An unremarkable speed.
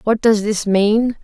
Yes: average, 195 wpm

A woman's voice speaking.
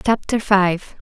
Yes: female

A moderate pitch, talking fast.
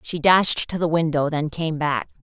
Yes: medium, 160 Hz; fast, 215 wpm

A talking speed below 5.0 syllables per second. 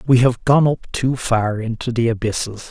Yes: 4.7 syllables/s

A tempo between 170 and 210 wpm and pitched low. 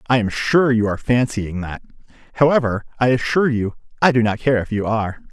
Yes: fast, 205 wpm; low, 115 Hz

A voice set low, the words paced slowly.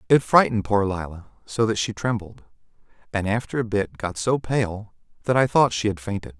No: low, 105 Hz; average, 195 wpm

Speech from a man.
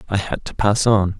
Yes: male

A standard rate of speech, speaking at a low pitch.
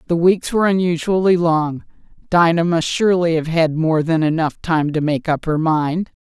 No: average, 185 wpm; medium, 165 Hz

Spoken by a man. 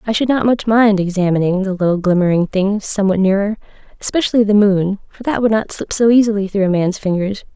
No: female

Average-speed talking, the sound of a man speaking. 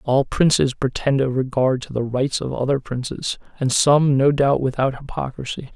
Yes: average, 175 wpm; male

